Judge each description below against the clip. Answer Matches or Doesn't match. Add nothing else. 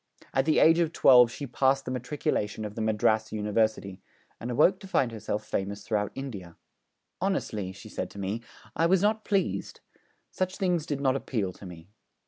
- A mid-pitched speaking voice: Doesn't match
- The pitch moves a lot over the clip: Matches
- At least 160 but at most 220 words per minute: Matches